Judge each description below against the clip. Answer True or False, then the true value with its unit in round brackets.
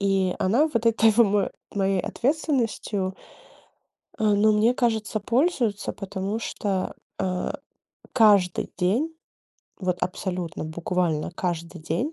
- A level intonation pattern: False (3.7 semitones)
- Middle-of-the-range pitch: False (200 Hz)